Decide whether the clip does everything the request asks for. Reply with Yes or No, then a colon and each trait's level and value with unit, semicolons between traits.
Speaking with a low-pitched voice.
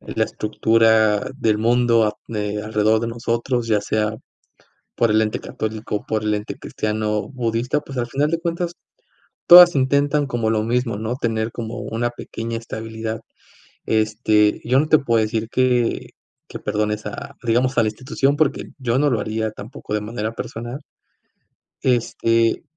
Yes: low, 115 Hz